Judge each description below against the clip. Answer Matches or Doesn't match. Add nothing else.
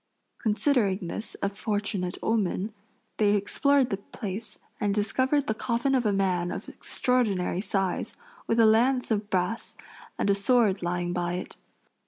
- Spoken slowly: Doesn't match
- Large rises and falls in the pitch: Doesn't match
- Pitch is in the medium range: Doesn't match